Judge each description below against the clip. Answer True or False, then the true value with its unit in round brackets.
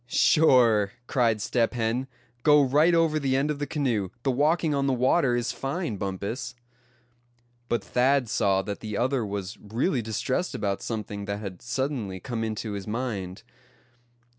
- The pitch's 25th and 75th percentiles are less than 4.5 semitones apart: False (4.9 semitones)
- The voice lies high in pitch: False (120 Hz)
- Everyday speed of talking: True (160 wpm)